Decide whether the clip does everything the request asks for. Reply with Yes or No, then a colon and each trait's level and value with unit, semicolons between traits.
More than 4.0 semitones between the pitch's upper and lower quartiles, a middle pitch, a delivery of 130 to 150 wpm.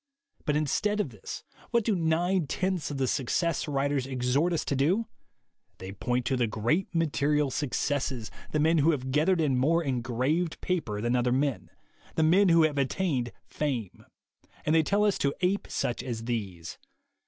No: average, 4.9 semitones; medium, 145 Hz; average, 175 wpm